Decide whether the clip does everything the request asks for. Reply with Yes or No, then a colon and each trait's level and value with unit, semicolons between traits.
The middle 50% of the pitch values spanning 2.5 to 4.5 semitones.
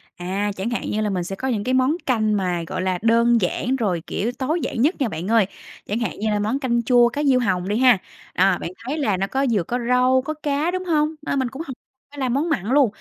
No: average, 4.9 semitones